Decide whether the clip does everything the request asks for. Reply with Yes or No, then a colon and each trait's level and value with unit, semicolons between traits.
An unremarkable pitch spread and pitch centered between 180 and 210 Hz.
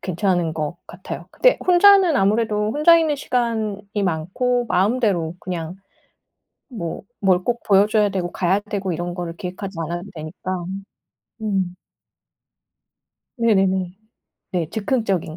Yes: average, 4.0 semitones; high, 195 Hz